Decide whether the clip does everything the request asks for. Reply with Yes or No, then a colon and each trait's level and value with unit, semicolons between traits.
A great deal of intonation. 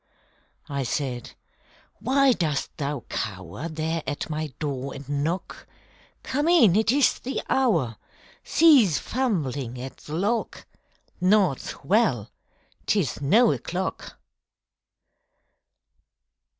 Yes: wide, 8.1 semitones